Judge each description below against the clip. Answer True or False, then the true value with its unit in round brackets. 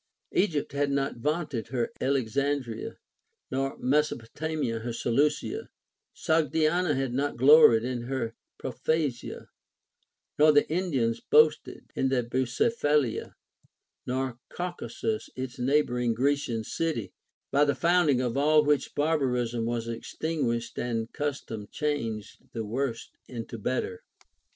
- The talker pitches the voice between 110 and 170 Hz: True (135 Hz)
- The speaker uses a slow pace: True (110 wpm)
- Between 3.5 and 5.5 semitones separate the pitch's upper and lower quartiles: True (4.1 semitones)